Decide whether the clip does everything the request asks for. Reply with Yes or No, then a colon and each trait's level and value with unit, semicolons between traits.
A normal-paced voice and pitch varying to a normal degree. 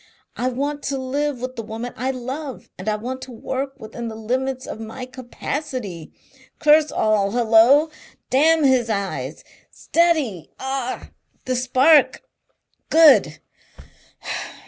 No: slow, 125 wpm; average, 3.5 semitones